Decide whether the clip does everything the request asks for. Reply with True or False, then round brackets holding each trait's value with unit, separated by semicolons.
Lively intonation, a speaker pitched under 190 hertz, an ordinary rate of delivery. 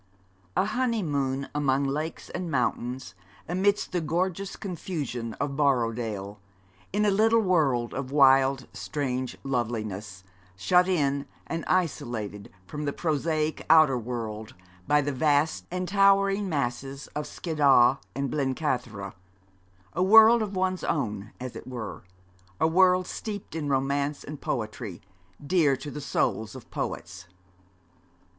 False (6.2 semitones; 140 Hz; 125 wpm)